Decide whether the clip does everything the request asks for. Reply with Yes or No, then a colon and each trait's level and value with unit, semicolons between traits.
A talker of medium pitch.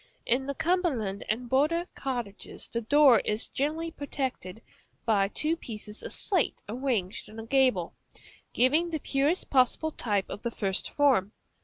No: very high, 255 Hz